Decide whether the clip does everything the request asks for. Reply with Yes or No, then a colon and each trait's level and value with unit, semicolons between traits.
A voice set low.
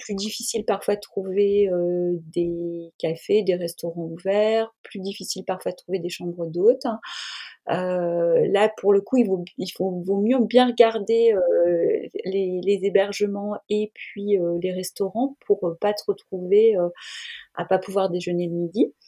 No: high, 195 Hz